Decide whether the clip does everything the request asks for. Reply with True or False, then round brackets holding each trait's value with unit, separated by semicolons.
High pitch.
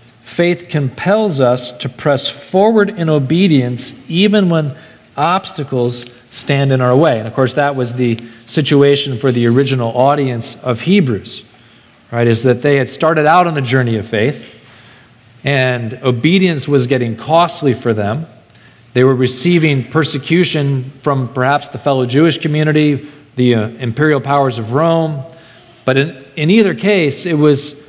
False (140 Hz)